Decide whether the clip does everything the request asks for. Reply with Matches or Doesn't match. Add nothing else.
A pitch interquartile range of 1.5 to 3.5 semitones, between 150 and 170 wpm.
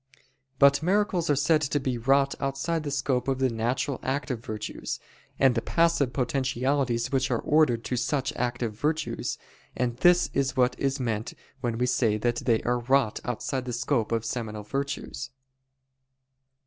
Matches